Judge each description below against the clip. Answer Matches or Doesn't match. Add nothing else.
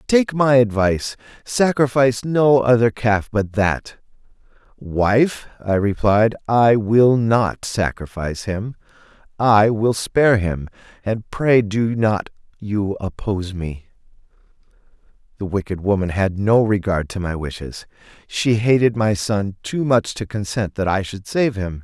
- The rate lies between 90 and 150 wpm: Matches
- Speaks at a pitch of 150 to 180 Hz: Doesn't match